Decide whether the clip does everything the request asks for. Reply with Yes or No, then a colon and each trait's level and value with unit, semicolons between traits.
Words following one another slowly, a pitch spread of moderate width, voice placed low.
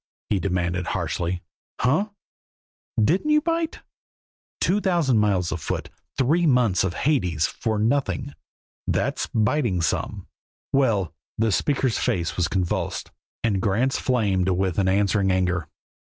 No: slow, 125 wpm; wide, 6.6 semitones; low, 105 Hz